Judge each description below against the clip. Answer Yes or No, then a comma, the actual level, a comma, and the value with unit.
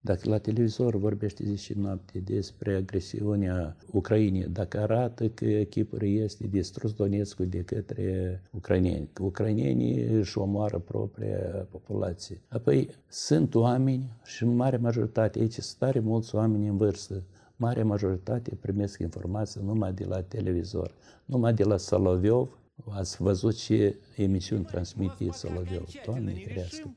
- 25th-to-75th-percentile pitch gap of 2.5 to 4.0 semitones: Yes, average, 2.9 semitones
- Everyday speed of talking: Yes, average, 130 wpm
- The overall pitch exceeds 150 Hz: No, low, 105 Hz